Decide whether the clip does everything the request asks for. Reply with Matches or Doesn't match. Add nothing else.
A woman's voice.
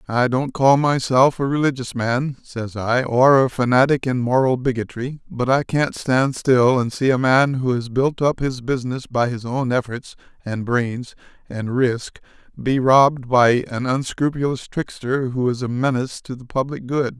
Doesn't match